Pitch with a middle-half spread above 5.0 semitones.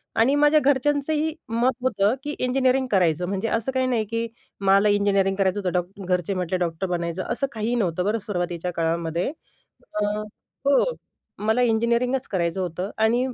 Yes: wide, 5.6 semitones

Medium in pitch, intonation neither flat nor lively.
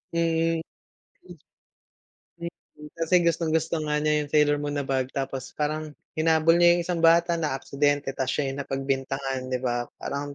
Yes: medium, 150 Hz; average, 3.2 semitones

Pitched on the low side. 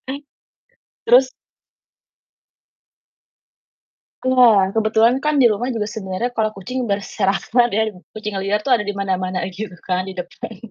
No: high, 215 Hz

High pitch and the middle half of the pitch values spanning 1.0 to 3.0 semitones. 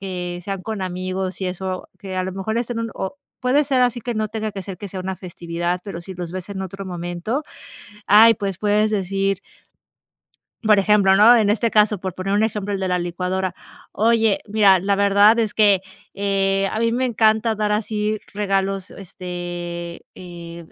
Yes: high, 195 Hz; average, 2.7 semitones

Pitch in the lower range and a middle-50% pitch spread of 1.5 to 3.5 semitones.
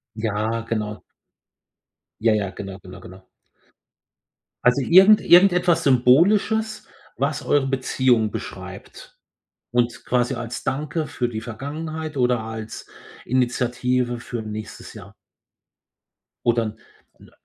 No: low, 125 Hz; average, 4.5 semitones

